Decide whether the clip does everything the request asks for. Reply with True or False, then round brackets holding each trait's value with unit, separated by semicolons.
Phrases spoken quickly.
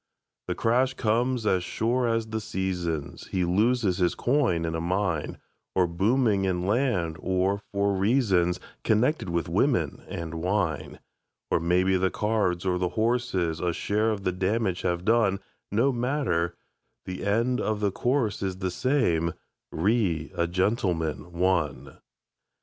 False (145 wpm)